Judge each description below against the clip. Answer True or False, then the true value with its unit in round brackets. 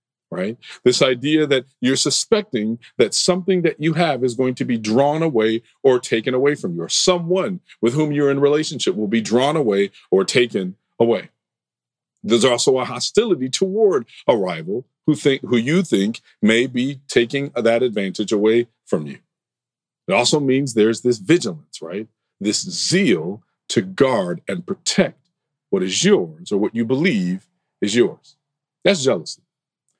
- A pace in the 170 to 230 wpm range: False (160 wpm)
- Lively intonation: True (6.5 semitones)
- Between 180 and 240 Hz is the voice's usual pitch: False (140 Hz)